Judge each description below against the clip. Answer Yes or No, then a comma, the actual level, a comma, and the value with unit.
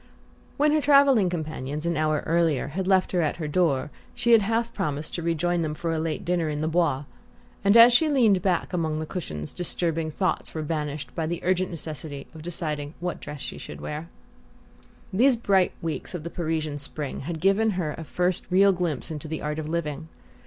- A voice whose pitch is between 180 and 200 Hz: No, medium, 165 Hz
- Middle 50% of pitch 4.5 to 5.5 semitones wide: No, average, 3.4 semitones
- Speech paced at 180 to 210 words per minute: Yes, average, 200 wpm